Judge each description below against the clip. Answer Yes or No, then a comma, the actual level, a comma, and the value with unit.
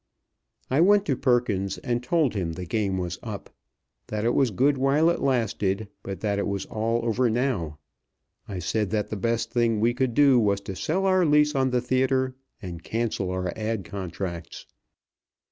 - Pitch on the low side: Yes, low, 115 Hz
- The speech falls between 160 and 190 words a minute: Yes, average, 180 wpm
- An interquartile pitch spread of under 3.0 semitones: No, average, 4.9 semitones